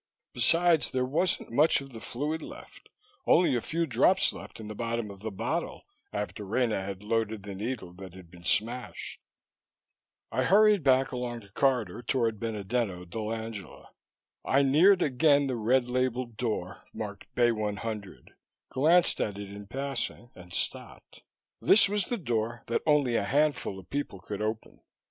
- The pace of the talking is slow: No, average, 160 wpm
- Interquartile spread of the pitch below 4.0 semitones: No, average, 4.8 semitones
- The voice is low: Yes, low, 120 Hz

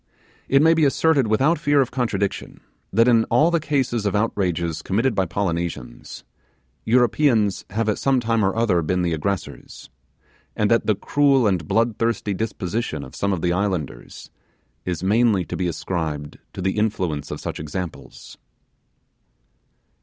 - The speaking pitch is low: Yes, low, 105 Hz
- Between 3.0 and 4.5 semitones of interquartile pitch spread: No, average, 5.1 semitones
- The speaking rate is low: No, average, 155 wpm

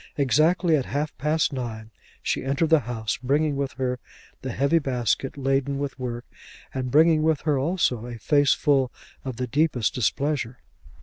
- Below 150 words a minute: No, average, 165 wpm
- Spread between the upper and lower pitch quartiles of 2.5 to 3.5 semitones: Yes, average, 3.2 semitones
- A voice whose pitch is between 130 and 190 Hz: Yes, low, 135 Hz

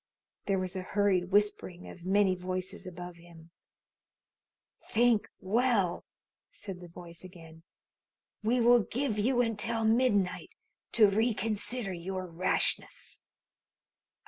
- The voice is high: Yes, high, 195 Hz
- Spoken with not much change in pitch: No, average, 3.8 semitones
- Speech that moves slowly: Yes, slow, 110 wpm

